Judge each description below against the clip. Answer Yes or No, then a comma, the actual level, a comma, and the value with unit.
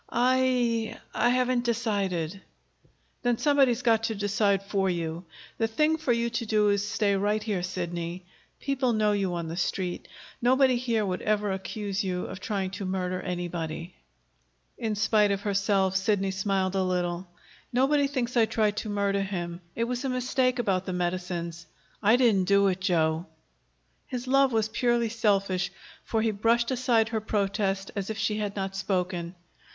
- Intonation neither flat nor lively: Yes, average, 3.8 semitones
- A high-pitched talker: Yes, high, 205 Hz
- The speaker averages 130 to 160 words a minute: No, average, 170 wpm